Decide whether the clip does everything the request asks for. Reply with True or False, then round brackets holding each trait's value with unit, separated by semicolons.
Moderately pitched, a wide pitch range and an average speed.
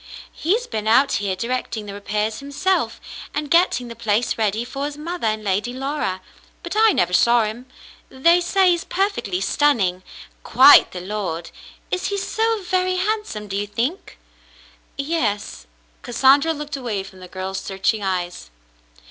False (235 Hz; 8.3 semitones; 160 wpm)